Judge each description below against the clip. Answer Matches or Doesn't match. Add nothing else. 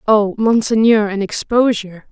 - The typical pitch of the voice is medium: Doesn't match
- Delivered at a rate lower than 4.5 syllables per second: Doesn't match